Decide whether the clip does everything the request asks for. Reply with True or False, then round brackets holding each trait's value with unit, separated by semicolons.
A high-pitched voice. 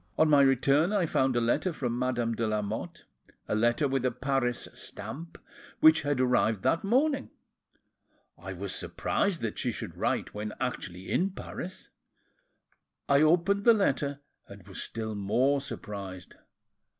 False (130 Hz)